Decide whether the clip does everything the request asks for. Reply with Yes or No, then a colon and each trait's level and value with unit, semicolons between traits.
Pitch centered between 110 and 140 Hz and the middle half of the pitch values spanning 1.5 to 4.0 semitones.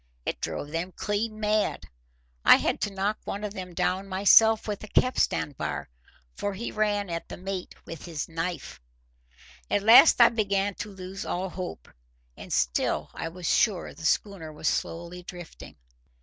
No: high, 190 Hz; average, 3.2 semitones